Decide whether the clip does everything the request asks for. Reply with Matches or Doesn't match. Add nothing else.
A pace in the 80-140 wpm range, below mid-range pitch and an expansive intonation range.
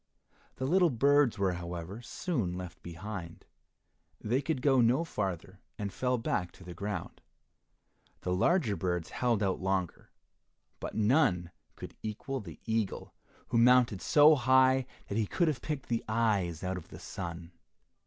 Doesn't match